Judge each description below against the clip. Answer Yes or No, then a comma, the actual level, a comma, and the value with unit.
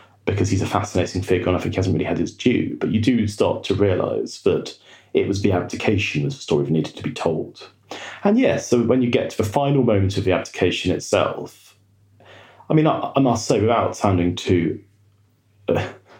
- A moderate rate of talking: No, fast, 210 wpm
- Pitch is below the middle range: Yes, low, 100 Hz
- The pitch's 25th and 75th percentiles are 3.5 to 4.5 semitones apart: No, average, 2.9 semitones